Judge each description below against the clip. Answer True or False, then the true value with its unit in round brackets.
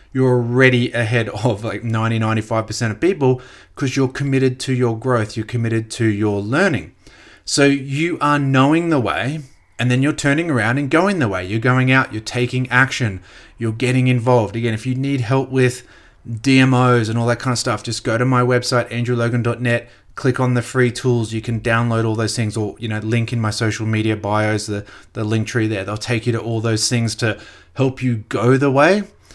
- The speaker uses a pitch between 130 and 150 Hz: False (120 Hz)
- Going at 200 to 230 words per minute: True (205 wpm)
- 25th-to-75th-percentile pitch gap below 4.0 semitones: True (2.5 semitones)